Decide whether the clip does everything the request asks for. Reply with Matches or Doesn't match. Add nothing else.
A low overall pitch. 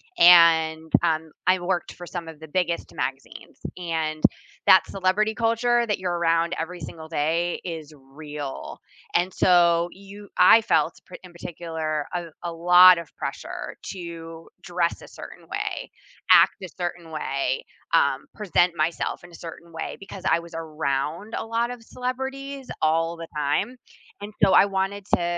Doesn't match